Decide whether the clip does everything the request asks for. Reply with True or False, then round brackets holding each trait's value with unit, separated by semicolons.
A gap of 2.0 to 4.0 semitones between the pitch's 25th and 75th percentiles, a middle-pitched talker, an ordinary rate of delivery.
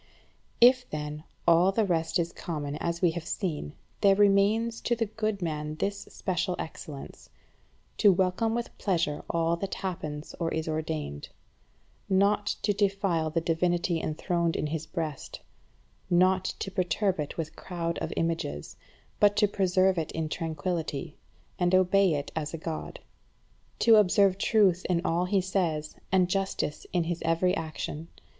True (3.4 semitones; 175 Hz; 155 wpm)